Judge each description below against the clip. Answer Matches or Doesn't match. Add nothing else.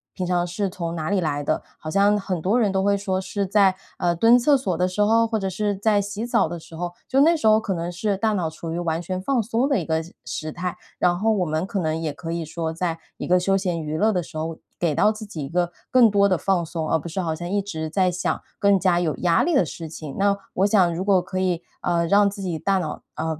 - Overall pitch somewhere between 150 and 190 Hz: Matches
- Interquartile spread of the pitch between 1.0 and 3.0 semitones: Doesn't match